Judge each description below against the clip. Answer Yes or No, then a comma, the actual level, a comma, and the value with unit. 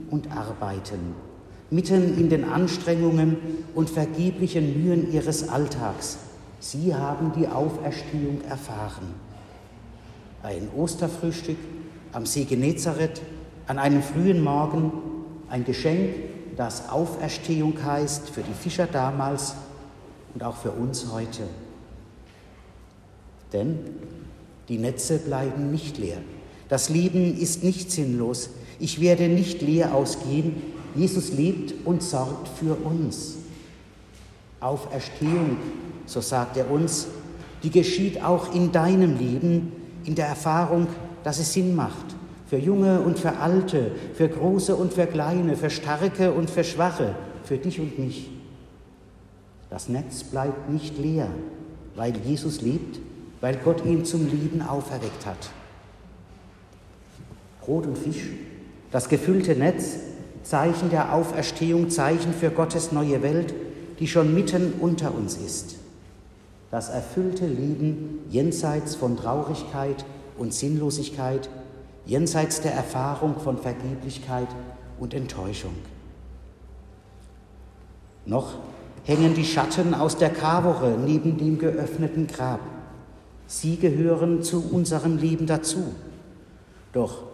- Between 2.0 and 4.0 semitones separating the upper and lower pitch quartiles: No, average, 4.7 semitones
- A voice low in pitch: No, medium, 150 Hz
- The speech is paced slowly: Yes, slow, 115 wpm